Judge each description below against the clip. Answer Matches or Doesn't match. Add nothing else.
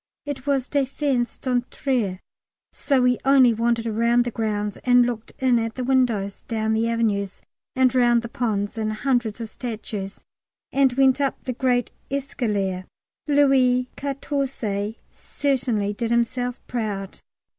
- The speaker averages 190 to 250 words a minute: Doesn't match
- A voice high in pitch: Matches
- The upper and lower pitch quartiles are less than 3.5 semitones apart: Matches